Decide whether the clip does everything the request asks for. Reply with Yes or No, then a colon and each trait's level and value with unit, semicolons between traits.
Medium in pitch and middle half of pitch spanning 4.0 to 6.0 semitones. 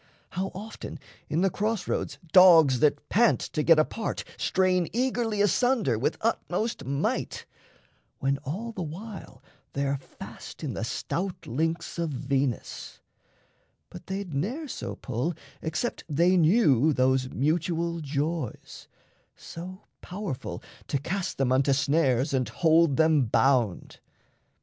Yes: medium, 165 Hz; wide, 5.5 semitones